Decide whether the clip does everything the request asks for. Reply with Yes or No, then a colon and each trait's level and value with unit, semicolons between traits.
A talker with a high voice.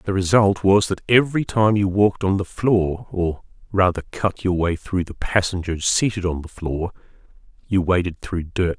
No: very low, 95 Hz